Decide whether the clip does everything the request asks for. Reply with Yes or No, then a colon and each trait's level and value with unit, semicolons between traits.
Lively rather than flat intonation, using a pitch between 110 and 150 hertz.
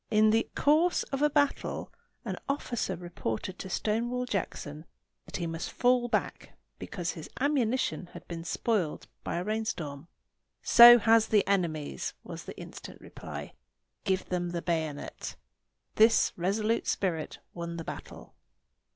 No: wide, 5.8 semitones; high, 195 Hz